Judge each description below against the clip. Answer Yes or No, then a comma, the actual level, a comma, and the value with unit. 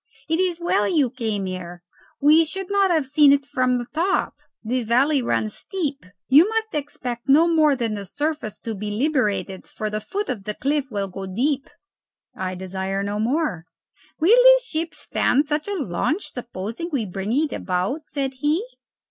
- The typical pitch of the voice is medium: No, very high, 270 Hz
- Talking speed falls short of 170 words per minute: No, average, 180 wpm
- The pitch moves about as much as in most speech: No, wide, 6.9 semitones